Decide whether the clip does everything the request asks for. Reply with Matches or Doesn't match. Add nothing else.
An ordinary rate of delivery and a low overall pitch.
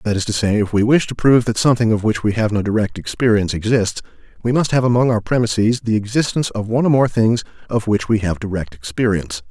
Doesn't match